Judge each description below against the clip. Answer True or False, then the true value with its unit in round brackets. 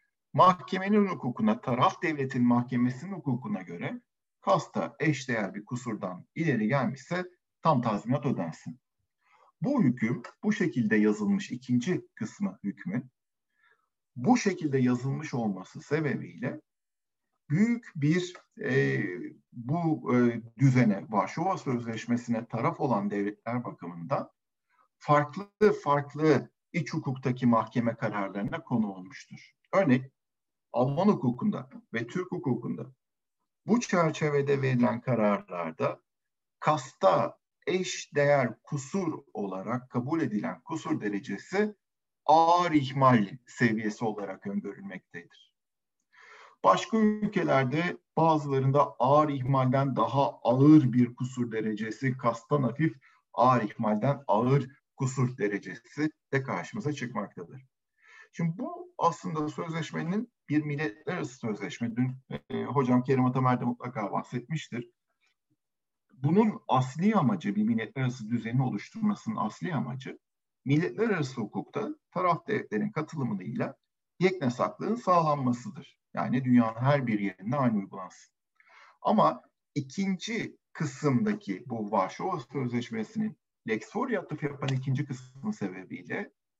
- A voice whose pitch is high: False (135 Hz)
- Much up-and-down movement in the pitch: True (6.1 semitones)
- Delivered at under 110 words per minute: True (100 wpm)